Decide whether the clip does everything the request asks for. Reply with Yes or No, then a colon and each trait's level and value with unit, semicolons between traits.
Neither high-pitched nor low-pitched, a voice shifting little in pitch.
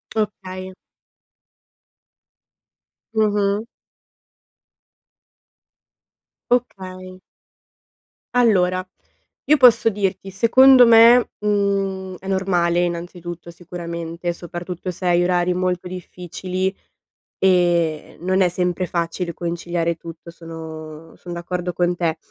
Yes: medium, 180 Hz; narrow, 2.0 semitones